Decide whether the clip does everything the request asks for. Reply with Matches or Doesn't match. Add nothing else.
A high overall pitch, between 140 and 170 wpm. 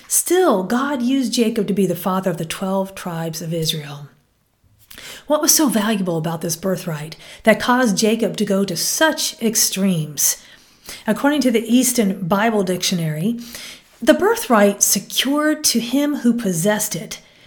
Matches